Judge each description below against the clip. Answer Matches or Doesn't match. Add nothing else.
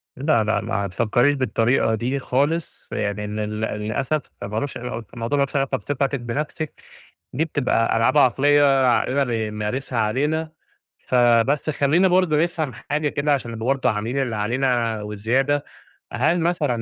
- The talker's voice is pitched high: Doesn't match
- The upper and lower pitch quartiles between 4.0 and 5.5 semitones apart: Matches